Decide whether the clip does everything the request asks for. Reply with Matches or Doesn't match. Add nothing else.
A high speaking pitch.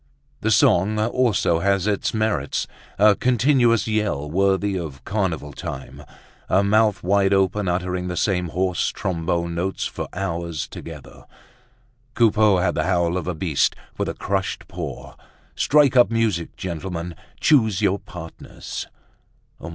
Doesn't match